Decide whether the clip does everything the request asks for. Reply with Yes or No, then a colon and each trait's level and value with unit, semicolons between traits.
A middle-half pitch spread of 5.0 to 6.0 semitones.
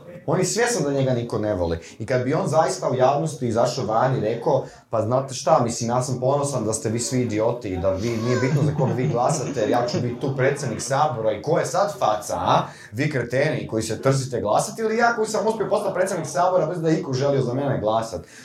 Yes: wide, 5.4 semitones